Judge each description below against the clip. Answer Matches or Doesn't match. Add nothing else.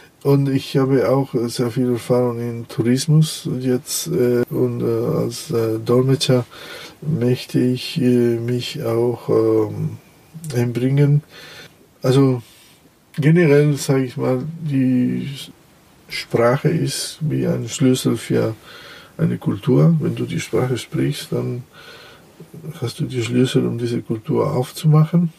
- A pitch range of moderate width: Matches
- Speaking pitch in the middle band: Doesn't match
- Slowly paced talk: Matches